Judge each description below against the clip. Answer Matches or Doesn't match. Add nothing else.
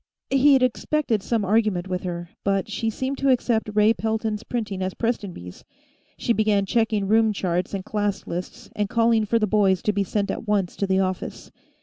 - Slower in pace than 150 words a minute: Doesn't match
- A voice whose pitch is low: Doesn't match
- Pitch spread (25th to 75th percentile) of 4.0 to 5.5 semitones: Doesn't match